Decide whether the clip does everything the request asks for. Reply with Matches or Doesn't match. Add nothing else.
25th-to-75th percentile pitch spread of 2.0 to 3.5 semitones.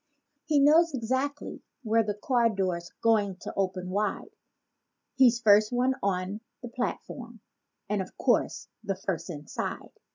Doesn't match